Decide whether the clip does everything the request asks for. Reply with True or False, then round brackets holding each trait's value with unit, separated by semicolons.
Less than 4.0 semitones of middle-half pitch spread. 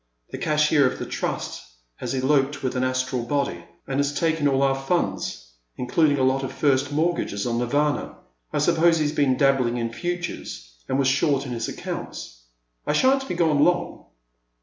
True (2.9 semitones)